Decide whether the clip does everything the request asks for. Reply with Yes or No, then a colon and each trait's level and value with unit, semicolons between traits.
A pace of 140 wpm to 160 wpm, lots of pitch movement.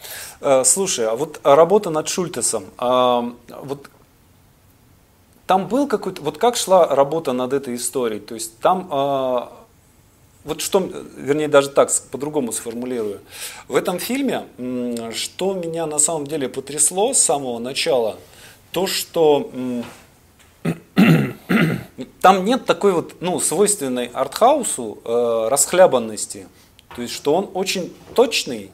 No: average, 115 wpm; wide, 7.3 semitones